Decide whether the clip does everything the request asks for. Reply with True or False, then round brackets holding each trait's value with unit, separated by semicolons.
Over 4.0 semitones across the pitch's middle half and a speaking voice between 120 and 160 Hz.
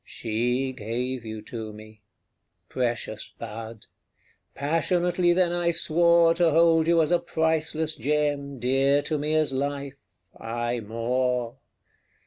True (5.5 semitones; 140 Hz)